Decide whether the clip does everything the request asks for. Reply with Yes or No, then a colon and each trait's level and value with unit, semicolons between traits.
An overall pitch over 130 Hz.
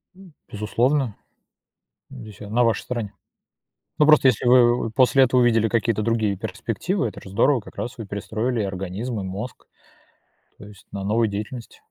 No: low, 115 Hz